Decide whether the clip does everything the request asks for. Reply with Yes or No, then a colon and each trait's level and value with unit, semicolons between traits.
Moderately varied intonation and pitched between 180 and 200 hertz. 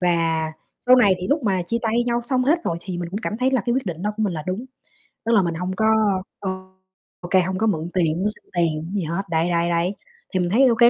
Yes: average, 4.9 semitones; high, 190 Hz